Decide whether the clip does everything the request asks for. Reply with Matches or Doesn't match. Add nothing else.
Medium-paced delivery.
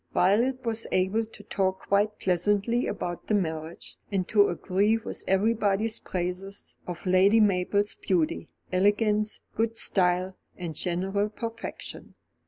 Doesn't match